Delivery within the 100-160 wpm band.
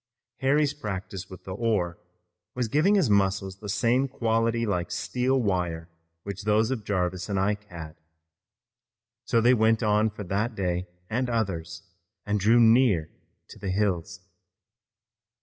Yes: average, 145 wpm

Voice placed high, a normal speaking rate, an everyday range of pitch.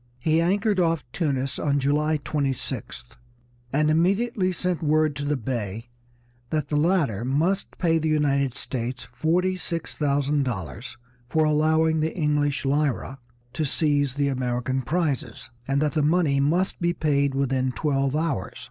No: medium, 145 Hz; average, 150 wpm; average, 3.0 semitones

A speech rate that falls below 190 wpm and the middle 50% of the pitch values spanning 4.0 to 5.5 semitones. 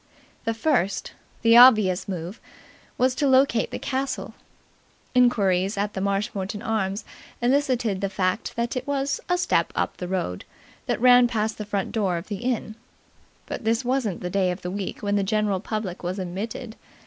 Yes: average, 170 wpm; average, 4.3 semitones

